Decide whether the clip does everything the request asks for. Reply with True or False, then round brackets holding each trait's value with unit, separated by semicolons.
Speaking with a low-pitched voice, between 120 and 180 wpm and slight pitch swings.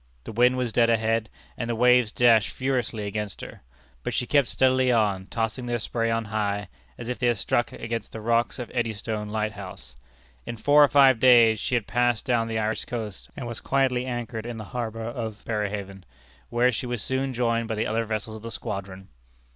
False (115 Hz; 205 wpm; 2.2 semitones)